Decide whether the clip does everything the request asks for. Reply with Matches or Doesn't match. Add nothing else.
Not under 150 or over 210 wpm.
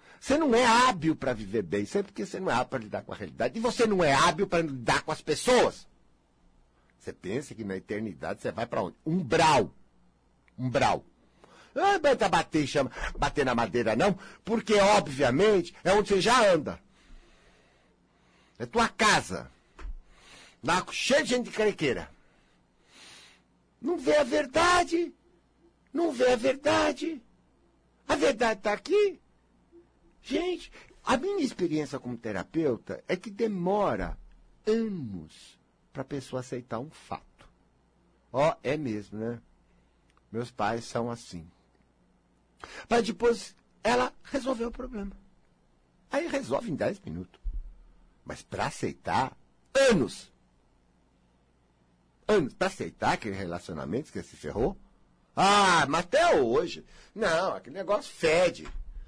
Doesn't match